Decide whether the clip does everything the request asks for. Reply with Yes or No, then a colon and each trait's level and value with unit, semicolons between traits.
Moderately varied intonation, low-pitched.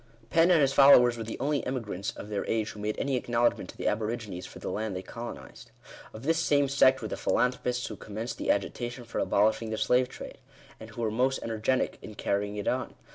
Yes: average, 3.4 semitones; low, 115 Hz